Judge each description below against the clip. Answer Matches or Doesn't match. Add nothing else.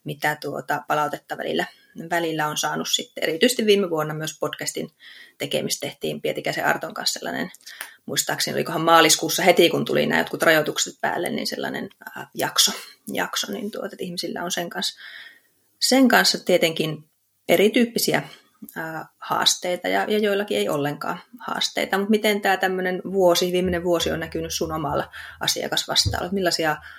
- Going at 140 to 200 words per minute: Matches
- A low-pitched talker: Doesn't match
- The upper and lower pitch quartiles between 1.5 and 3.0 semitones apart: Doesn't match